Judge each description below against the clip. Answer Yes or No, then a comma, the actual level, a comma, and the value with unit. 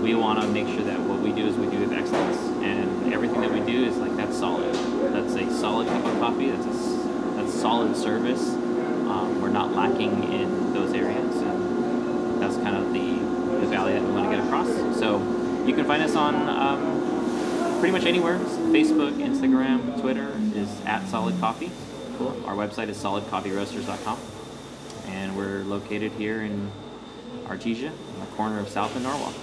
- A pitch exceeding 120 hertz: No, low, 110 Hz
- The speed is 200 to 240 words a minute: No, average, 180 wpm